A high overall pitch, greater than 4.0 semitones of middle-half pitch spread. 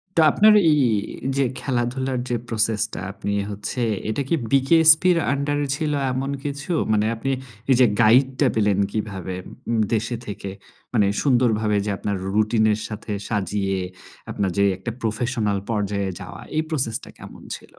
No: low, 115 Hz; average, 4.4 semitones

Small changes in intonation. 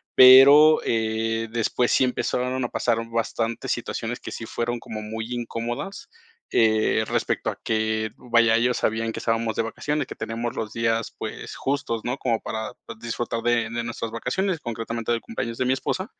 Yes: narrow, 1.6 semitones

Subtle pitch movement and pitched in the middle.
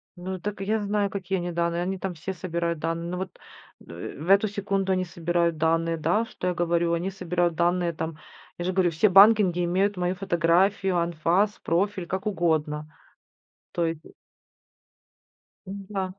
Yes: narrow, 2.3 semitones; medium, 175 Hz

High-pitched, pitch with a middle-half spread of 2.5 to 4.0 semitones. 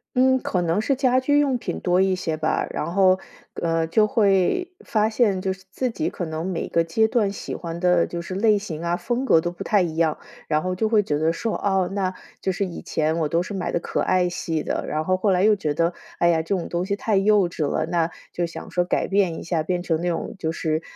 No: medium, 180 Hz; average, 3.6 semitones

